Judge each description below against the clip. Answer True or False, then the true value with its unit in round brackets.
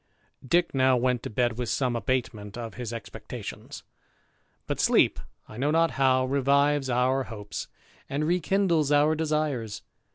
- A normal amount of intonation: True (3.5 semitones)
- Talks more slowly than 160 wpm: True (140 wpm)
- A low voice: True (130 Hz)